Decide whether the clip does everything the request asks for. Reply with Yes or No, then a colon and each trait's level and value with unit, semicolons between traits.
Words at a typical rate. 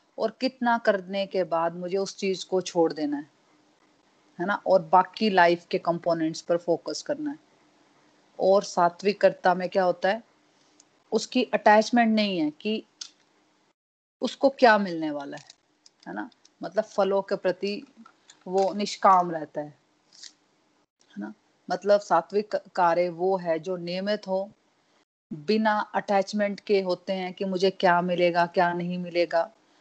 Yes: average, 145 wpm